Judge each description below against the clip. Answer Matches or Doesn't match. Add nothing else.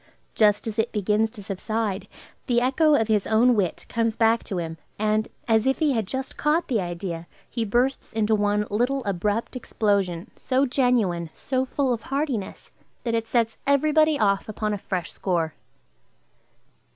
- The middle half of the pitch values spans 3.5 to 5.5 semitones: Matches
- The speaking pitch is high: Matches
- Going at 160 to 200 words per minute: Matches